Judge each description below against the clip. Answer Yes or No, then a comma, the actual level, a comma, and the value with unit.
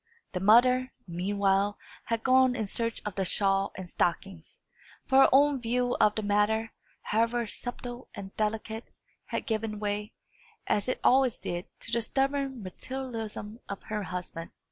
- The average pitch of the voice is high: Yes, high, 220 Hz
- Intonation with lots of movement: No, average, 3.7 semitones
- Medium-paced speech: Yes, average, 150 wpm